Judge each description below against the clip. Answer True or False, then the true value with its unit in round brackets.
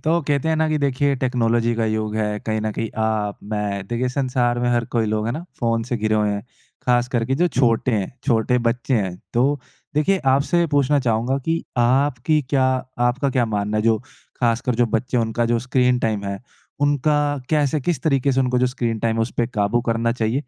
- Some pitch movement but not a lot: True (3.3 semitones)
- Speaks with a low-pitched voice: True (120 Hz)